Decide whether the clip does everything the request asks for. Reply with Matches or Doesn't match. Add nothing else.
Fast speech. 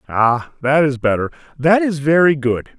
Doesn't match